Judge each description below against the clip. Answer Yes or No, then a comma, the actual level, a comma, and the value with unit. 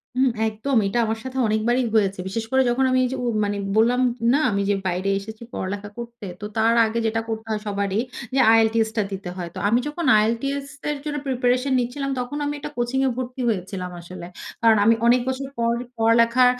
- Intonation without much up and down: No, average, 3.2 semitones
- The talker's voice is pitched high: Yes, high, 230 Hz